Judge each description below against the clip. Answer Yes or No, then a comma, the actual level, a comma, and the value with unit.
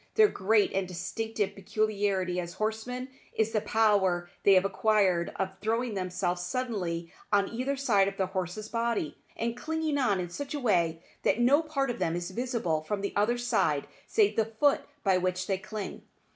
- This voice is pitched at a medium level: No, high, 205 Hz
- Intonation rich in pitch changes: No, average, 4.3 semitones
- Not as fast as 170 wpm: No, average, 180 wpm